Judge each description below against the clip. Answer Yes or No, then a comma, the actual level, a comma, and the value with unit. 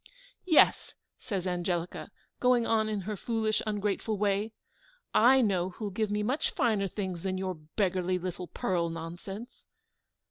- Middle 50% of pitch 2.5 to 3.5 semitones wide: Yes, average, 3.1 semitones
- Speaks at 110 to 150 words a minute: Yes, average, 140 wpm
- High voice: Yes, high, 200 Hz